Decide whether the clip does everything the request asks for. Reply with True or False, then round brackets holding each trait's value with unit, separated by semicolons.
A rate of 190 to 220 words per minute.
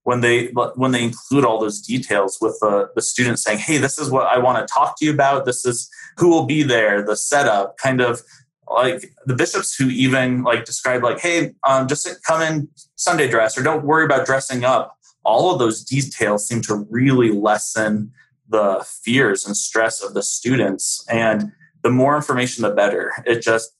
True (200 wpm)